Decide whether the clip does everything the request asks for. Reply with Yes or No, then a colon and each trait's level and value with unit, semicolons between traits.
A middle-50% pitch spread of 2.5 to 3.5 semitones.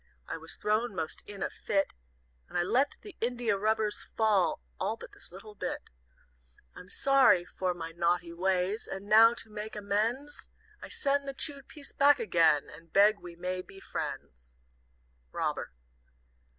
No: average, 4.7 semitones